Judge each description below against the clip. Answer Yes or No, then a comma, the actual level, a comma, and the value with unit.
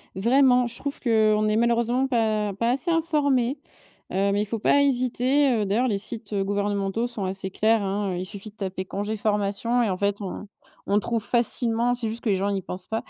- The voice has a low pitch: No, high, 220 Hz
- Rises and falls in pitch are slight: No, average, 3.2 semitones